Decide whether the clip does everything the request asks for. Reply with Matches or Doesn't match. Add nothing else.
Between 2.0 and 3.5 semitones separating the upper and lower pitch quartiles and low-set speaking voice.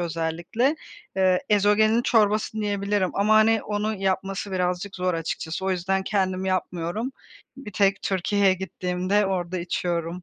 Doesn't match